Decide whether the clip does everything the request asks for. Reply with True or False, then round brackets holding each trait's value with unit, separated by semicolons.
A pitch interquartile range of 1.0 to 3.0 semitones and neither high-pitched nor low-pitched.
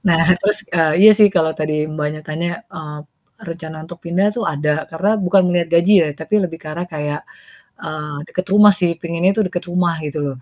True (2.6 semitones; 165 Hz)